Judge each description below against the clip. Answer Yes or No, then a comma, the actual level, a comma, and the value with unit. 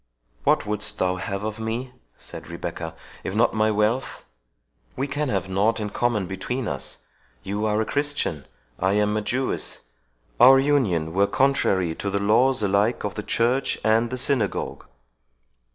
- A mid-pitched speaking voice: No, low, 105 Hz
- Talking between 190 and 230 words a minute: No, average, 145 wpm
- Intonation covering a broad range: No, average, 4.3 semitones